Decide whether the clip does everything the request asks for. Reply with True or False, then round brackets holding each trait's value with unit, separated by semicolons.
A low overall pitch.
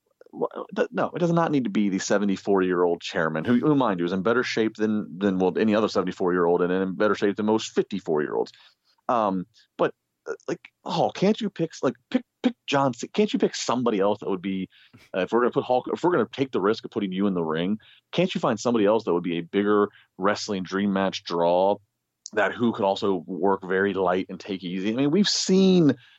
True (100 Hz)